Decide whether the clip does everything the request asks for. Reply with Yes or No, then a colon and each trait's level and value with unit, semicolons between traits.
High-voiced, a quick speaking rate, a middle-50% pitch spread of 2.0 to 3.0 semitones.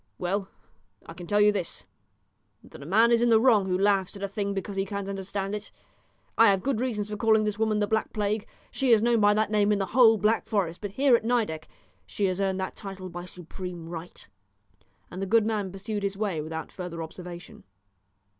Yes: high, 200 Hz; fast, 220 wpm; narrow, 2.6 semitones